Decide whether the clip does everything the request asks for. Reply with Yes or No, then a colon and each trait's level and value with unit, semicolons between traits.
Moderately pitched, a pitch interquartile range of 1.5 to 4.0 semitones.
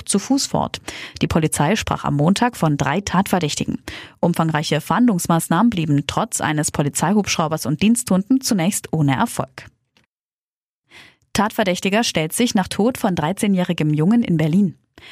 No: medium, 180 Hz; wide, 5.4 semitones